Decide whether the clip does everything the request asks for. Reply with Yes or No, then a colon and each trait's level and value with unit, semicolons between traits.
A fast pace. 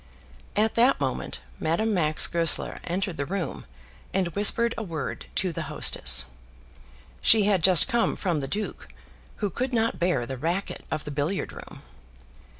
No: average, 155 wpm